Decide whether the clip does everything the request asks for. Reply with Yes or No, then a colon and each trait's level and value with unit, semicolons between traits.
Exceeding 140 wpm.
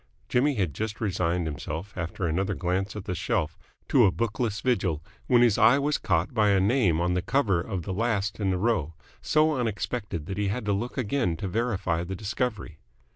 Yes: average, 200 wpm